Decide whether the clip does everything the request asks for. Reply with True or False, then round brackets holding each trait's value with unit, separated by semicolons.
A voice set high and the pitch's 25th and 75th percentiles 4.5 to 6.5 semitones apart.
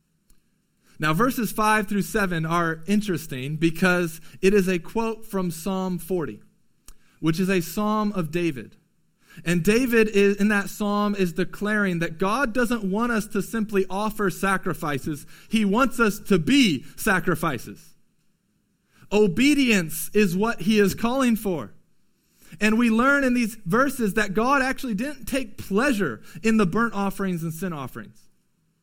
False (200 Hz; 4.0 semitones)